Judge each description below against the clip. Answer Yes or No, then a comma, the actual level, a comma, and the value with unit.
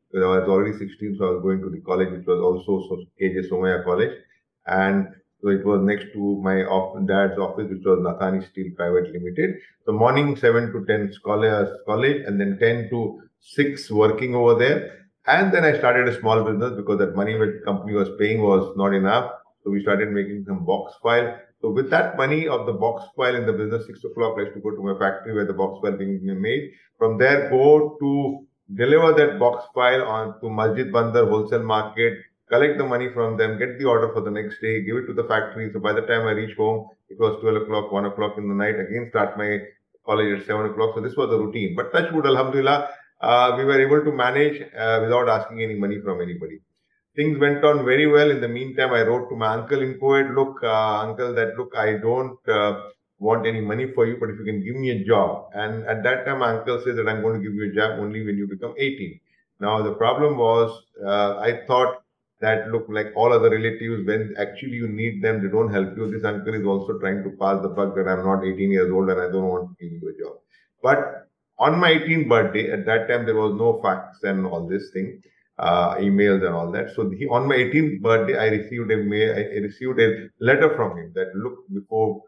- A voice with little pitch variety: No, average, 3.7 semitones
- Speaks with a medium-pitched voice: No, low, 110 Hz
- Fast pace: Yes, fast, 230 wpm